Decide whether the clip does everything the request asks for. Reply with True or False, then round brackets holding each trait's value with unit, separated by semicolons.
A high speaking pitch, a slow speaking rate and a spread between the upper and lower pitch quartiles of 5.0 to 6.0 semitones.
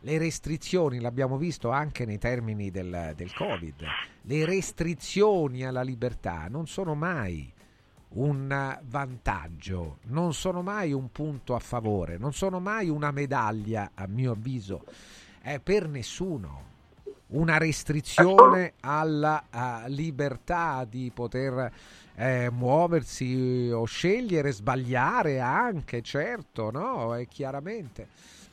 False (130 Hz; 110 wpm; 5.3 semitones)